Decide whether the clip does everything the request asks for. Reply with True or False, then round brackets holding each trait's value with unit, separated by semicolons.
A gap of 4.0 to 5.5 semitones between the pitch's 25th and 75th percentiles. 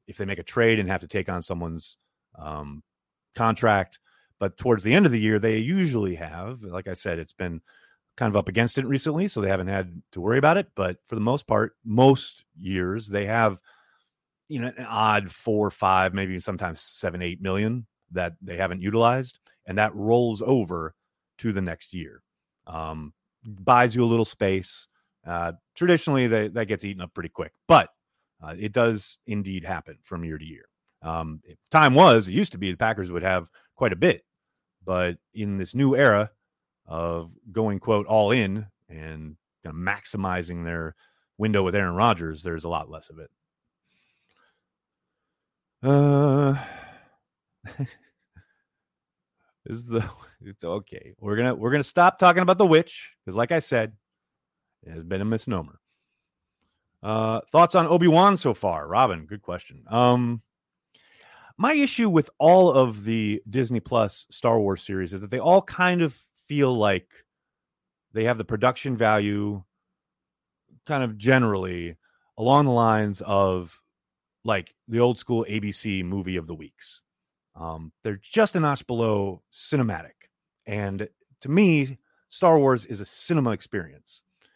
True (5.0 semitones)